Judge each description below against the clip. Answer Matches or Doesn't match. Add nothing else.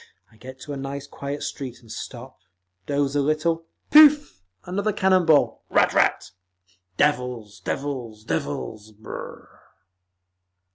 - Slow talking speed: Matches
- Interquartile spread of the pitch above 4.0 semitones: Matches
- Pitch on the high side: Doesn't match